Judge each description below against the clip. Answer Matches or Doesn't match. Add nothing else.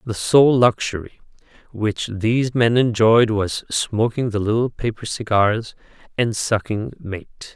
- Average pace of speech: Doesn't match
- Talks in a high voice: Doesn't match